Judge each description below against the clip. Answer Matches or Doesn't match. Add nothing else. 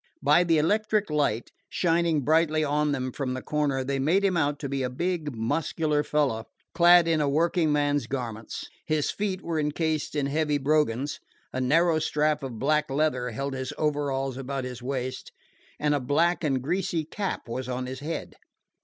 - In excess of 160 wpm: Matches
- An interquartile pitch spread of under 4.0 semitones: Matches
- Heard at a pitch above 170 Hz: Doesn't match